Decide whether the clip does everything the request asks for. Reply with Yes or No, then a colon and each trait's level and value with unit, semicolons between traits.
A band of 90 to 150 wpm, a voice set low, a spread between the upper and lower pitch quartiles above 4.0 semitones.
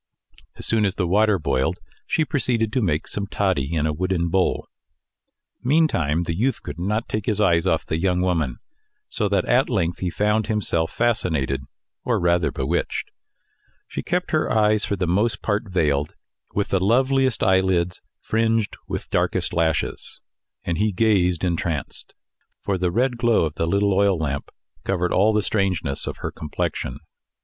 No: average, 165 wpm; very low, 95 Hz; average, 4.4 semitones